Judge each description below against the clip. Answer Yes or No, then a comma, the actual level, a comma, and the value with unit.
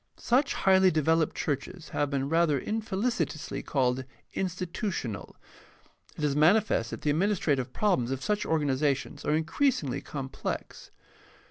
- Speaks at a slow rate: Yes, slow, 120 wpm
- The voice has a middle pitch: Yes, medium, 160 Hz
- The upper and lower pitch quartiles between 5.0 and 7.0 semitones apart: Yes, wide, 5.6 semitones